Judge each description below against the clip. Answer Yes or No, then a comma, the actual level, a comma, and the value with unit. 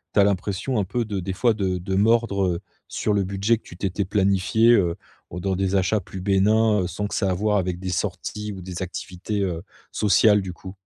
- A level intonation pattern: Yes, narrow, 2.3 semitones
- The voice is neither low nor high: No, very low, 95 Hz